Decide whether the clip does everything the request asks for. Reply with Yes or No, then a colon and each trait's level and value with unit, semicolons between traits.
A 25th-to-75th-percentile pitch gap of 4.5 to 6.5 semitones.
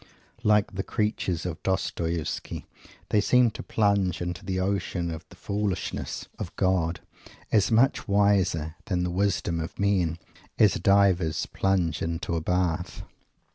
No: average, 2.9 semitones